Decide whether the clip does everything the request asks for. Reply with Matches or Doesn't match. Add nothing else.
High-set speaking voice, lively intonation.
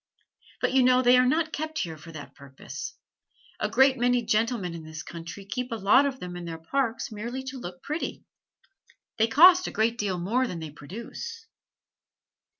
Matches